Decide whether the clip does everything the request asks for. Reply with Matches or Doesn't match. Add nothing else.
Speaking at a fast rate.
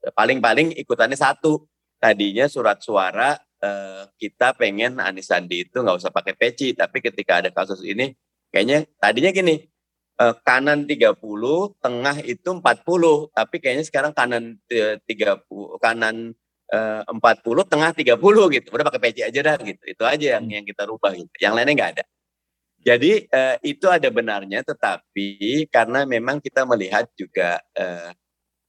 Matches